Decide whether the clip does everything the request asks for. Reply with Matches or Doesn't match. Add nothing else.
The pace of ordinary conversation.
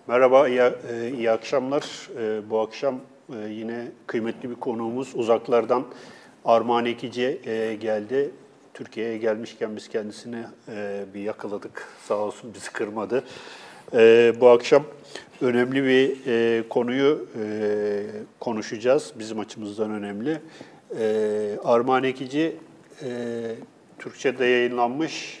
Doesn't match